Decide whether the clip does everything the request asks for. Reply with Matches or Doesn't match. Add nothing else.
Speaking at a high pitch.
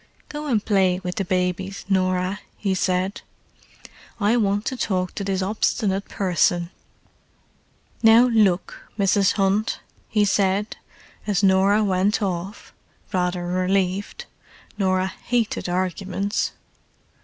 Matches